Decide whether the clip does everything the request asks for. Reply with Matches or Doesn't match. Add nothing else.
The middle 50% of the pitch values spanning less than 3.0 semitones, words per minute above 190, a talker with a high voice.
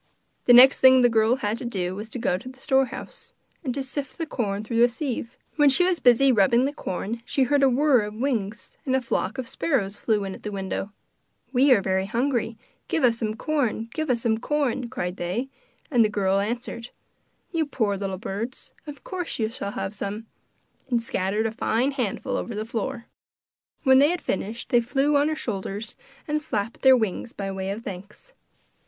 Doesn't match